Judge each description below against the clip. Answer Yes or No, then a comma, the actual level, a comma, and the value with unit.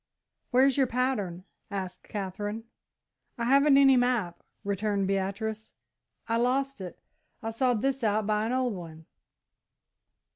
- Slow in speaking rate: Yes, slow, 125 wpm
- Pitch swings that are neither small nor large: Yes, average, 4.4 semitones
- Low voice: No, high, 220 Hz